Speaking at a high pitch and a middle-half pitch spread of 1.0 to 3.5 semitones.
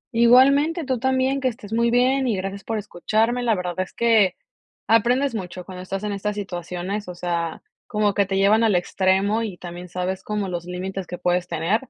No: high, 200 Hz; average, 4.3 semitones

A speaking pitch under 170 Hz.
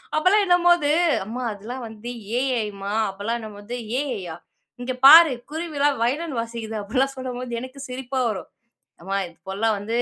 No: very high, 250 Hz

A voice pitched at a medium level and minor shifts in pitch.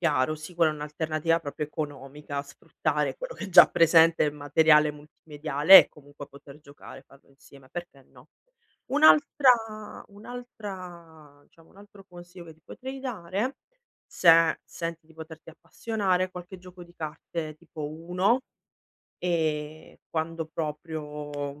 No: medium, 160 Hz; average, 3.3 semitones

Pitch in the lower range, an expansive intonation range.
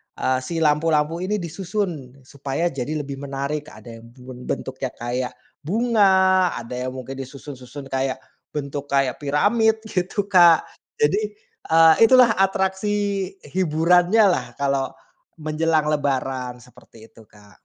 No: medium, 150 Hz; wide, 5.9 semitones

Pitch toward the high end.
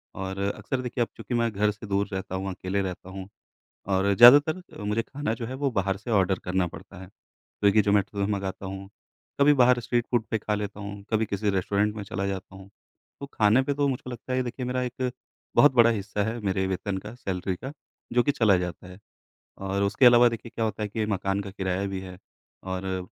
No: low, 105 Hz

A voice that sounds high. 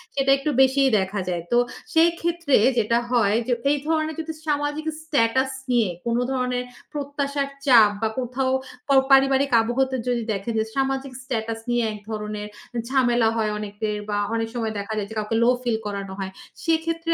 Yes: high, 245 Hz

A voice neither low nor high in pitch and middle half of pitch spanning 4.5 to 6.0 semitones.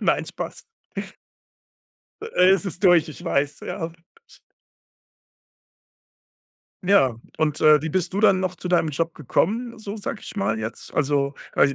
Yes: medium, 170 Hz; average, 4.9 semitones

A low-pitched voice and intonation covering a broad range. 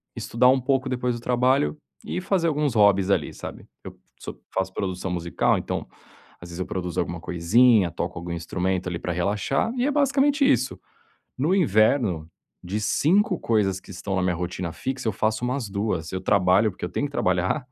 Yes: low, 105 Hz; wide, 6.7 semitones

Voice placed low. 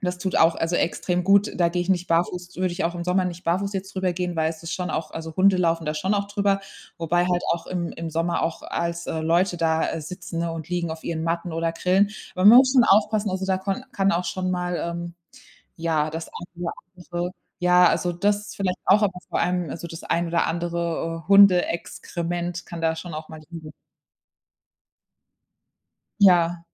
No: medium, 175 Hz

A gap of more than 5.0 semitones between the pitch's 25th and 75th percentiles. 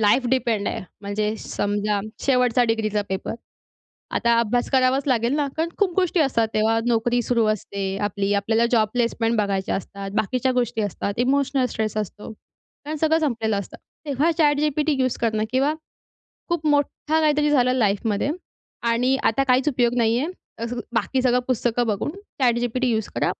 No: average, 3.7 semitones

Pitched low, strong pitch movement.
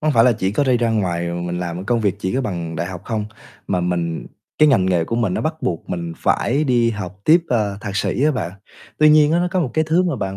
Yes: low, 105 Hz; wide, 7.4 semitones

